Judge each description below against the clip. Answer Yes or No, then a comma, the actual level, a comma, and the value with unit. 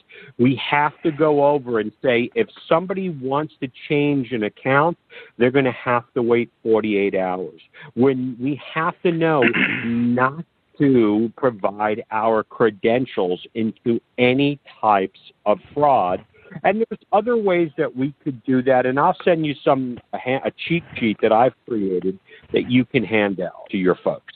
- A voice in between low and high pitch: No, low, 130 Hz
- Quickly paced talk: No, average, 165 wpm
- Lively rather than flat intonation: No, average, 4.7 semitones